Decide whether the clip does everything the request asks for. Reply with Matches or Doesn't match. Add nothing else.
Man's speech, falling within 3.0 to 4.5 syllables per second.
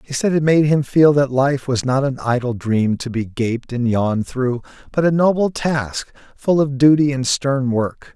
Matches